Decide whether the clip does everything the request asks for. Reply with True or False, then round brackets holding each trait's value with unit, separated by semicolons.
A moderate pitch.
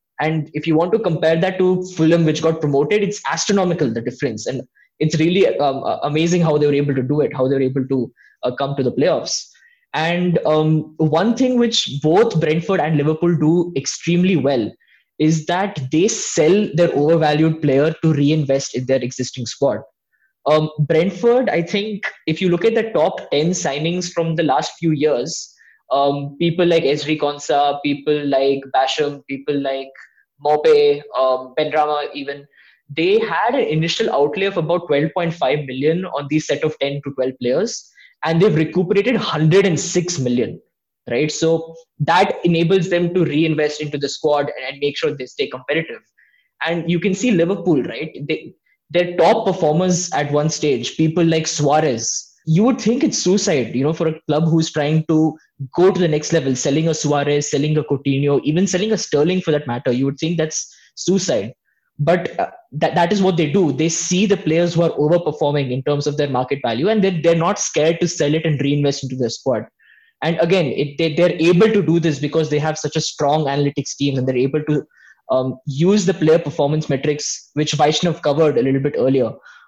True (155 Hz)